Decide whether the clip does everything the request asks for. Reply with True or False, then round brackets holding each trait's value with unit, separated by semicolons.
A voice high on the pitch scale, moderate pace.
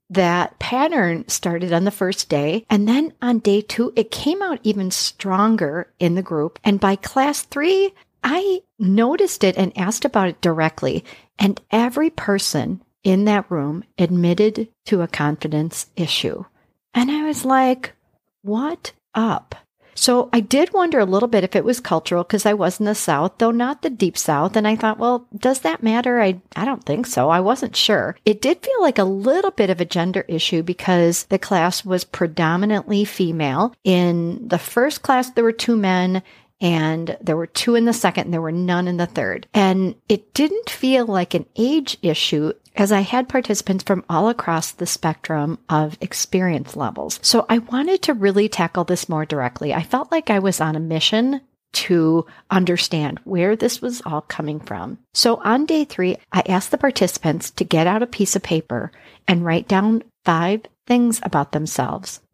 True (195 Hz; 185 wpm)